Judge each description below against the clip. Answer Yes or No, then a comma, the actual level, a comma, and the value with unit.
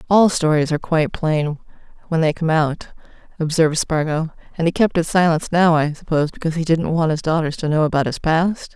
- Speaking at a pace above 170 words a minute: Yes, average, 190 wpm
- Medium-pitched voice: Yes, medium, 160 Hz